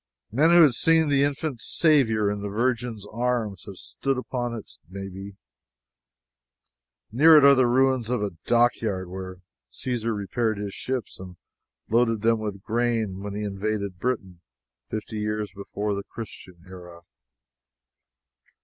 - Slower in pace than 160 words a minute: Yes, average, 140 wpm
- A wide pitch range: No, average, 3.9 semitones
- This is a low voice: Yes, low, 110 Hz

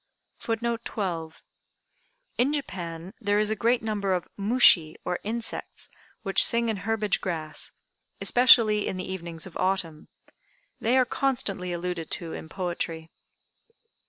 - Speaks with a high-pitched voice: Yes, high, 195 Hz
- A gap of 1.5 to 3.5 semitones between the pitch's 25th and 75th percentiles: No, average, 4.7 semitones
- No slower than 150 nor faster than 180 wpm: No, slow, 135 wpm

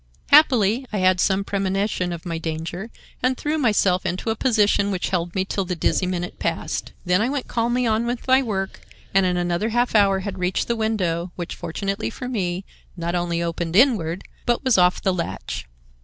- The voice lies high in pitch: Yes, high, 195 Hz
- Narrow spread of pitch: No, average, 4.3 semitones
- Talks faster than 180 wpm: Yes, average, 195 wpm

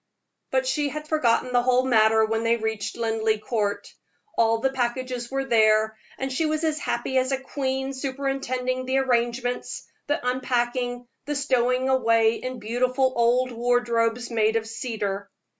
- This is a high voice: Yes, high, 245 Hz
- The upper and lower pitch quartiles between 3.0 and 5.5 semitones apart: No, narrow, 2.5 semitones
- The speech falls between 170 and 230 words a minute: No, average, 155 wpm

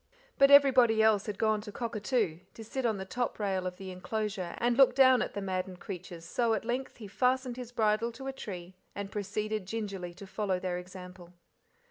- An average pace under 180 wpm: No, average, 200 wpm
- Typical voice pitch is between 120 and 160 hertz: No, high, 210 Hz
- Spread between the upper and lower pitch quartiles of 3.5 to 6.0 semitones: Yes, average, 4.2 semitones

